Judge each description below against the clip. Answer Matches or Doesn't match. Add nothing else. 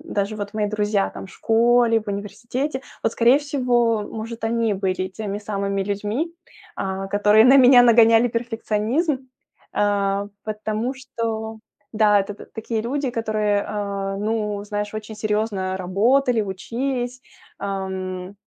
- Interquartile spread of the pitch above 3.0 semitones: Doesn't match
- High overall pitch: Matches